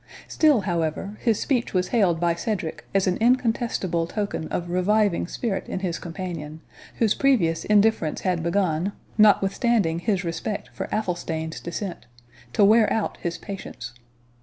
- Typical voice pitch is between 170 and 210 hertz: Yes, medium, 185 Hz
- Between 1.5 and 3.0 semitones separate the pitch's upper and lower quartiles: No, average, 4.1 semitones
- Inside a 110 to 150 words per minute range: Yes, average, 140 wpm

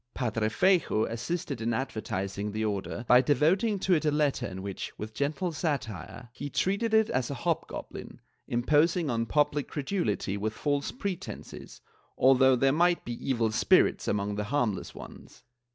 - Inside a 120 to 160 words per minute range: Yes, average, 155 wpm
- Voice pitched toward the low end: Yes, low, 130 Hz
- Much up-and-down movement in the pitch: Yes, wide, 6.1 semitones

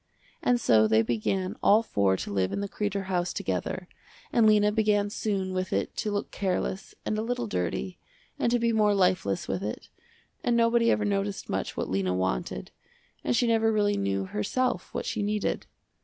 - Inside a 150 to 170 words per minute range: No, average, 185 wpm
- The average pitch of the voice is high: Yes, high, 195 Hz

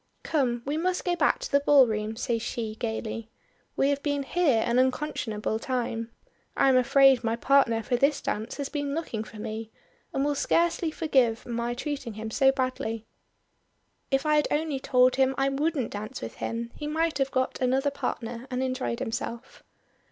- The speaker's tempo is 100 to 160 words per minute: No, average, 180 wpm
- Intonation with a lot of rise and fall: No, average, 3.7 semitones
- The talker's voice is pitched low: No, very high, 260 Hz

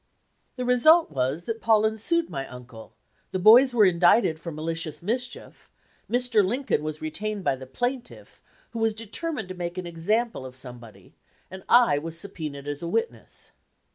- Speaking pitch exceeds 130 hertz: Yes, medium, 185 Hz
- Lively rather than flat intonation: Yes, wide, 7.3 semitones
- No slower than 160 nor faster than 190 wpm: Yes, average, 170 wpm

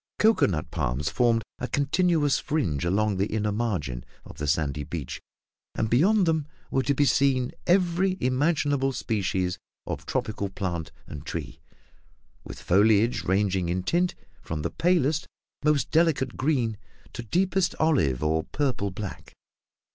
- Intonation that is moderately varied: No, wide, 8.5 semitones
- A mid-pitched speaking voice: No, low, 115 Hz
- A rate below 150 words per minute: Yes, average, 140 wpm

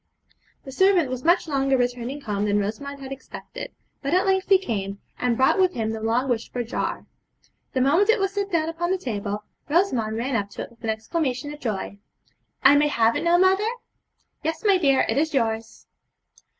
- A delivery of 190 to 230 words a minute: Yes, average, 200 wpm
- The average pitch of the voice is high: Yes, very high, 270 Hz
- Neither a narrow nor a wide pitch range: No, wide, 7.0 semitones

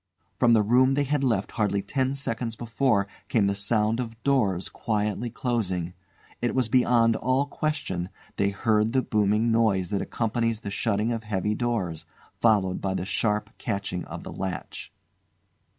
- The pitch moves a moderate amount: Yes, average, 3.2 semitones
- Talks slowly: No, average, 160 wpm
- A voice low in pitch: Yes, low, 110 Hz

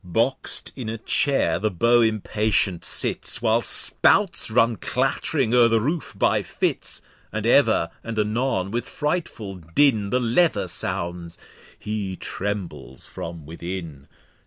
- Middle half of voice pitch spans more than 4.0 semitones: Yes, average, 4.8 semitones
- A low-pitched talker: Yes, low, 110 Hz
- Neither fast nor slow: No, slow, 130 wpm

